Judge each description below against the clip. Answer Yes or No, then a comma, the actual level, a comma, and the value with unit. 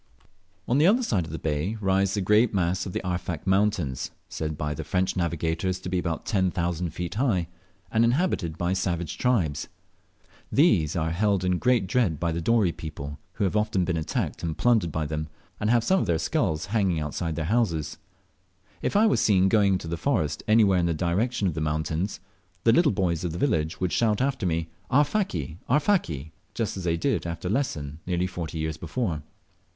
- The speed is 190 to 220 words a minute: Yes, average, 200 wpm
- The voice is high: No, very low, 90 Hz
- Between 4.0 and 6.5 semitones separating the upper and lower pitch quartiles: Yes, average, 4.9 semitones